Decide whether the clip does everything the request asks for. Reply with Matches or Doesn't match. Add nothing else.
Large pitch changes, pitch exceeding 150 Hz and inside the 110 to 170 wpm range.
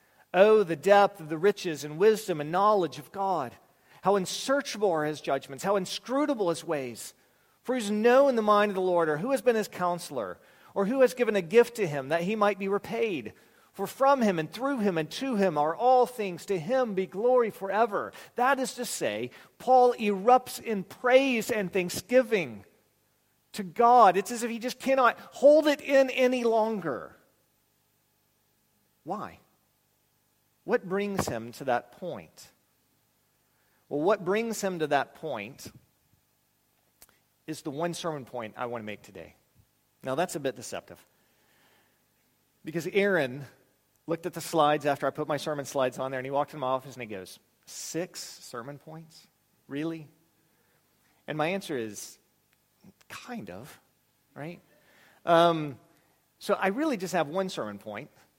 Matches